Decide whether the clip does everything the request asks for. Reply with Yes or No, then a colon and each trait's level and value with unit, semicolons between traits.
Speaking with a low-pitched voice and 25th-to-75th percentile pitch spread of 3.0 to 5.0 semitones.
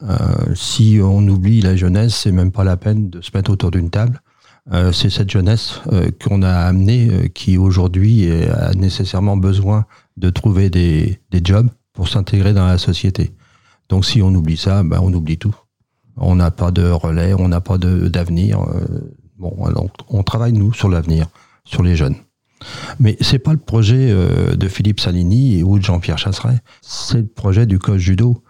Yes: low, 100 Hz; average, 3.7 semitones